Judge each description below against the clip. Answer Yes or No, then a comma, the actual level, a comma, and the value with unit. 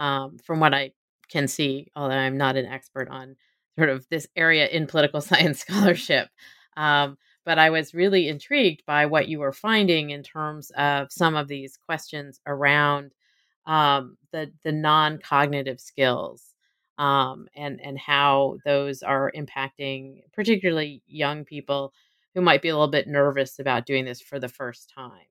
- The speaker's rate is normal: Yes, average, 160 wpm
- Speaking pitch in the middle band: Yes, medium, 145 Hz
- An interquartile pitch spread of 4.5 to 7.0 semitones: No, narrow, 2.5 semitones